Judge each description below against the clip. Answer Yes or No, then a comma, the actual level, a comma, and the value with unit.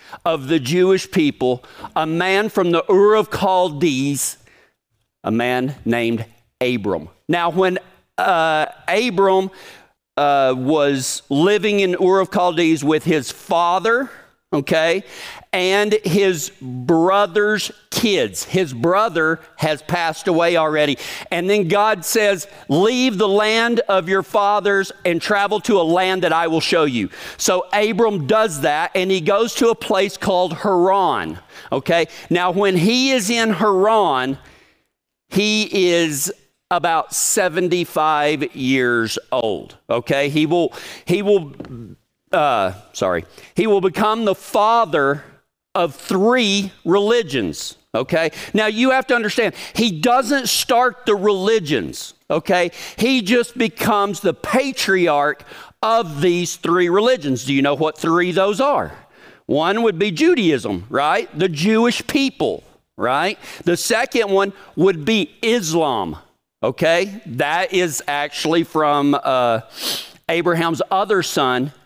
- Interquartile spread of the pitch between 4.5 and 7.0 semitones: Yes, average, 5.0 semitones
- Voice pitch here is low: No, medium, 185 Hz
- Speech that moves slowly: Yes, slow, 125 wpm